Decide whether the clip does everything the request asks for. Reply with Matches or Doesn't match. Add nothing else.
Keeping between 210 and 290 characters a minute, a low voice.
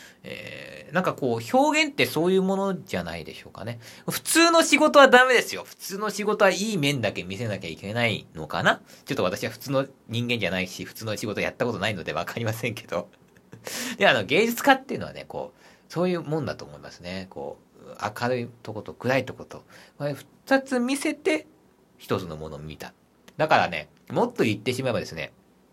Doesn't match